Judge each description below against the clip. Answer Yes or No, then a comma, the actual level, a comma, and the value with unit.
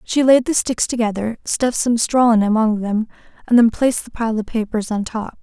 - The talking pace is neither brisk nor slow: No, fast, 220 wpm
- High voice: Yes, high, 225 Hz